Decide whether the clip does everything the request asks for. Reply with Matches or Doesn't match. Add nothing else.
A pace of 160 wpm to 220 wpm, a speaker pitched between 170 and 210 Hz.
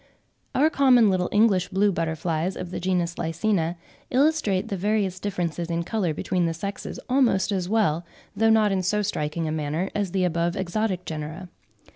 Matches